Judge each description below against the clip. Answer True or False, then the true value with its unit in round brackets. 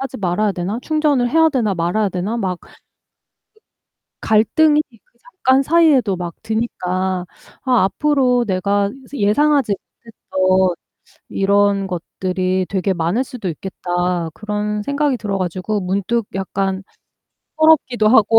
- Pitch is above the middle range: True (205 Hz)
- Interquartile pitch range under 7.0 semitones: True (5.1 semitones)